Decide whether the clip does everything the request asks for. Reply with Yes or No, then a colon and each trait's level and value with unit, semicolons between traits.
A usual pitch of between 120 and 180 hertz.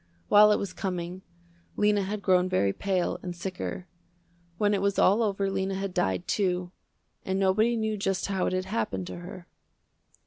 No: high, 190 Hz